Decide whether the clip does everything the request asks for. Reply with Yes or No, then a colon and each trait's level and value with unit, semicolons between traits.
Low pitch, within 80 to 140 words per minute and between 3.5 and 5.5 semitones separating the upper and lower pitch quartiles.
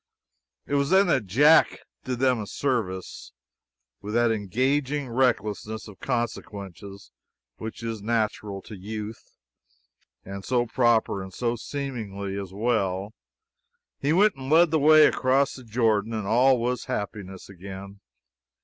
Yes: low, 115 Hz; slow, 135 wpm; average, 4.6 semitones